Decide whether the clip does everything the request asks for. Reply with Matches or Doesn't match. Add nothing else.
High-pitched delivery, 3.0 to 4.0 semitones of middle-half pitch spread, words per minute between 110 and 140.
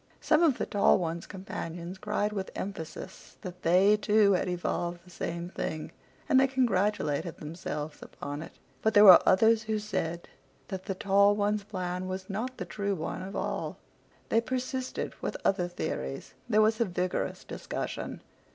Doesn't match